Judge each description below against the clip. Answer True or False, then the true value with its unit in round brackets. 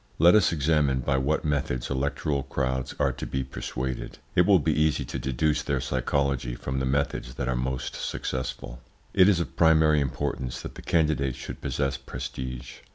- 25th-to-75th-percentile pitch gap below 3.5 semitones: True (2.9 semitones)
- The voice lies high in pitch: False (70 Hz)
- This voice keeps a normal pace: True (175 wpm)